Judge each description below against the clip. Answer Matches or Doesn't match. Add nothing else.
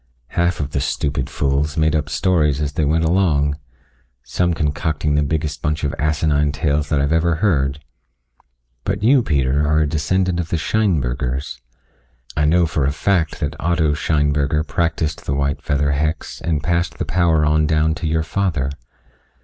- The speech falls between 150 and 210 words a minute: Matches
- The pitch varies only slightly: Matches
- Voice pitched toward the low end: Matches